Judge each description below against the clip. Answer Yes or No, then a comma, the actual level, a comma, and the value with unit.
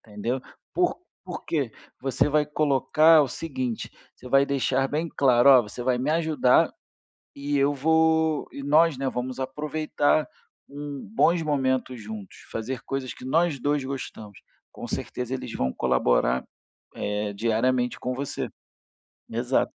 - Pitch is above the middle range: No, low, 135 Hz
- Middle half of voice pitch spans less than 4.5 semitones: Yes, average, 3.2 semitones